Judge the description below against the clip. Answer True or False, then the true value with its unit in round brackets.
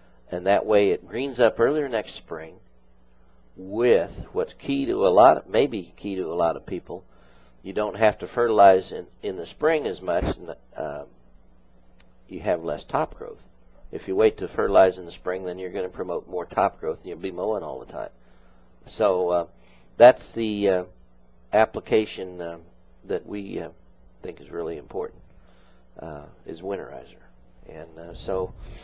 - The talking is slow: False (175 wpm)